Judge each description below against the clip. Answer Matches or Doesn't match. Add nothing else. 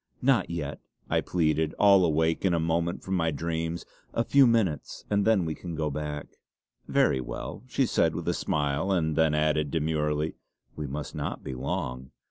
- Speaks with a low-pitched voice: Matches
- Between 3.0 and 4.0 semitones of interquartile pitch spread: Doesn't match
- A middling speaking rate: Matches